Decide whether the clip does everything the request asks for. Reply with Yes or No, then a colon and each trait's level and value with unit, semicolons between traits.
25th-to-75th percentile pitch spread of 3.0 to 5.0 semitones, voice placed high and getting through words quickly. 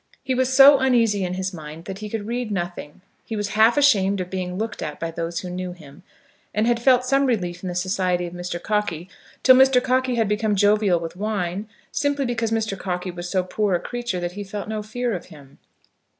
Yes: average, 4.7 semitones; high, 205 Hz; fast, 220 wpm